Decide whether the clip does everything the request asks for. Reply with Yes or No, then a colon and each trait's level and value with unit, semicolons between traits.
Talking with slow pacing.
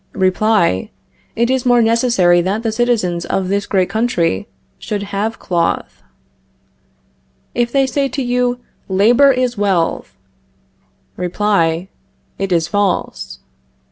Yes: slow, 115 wpm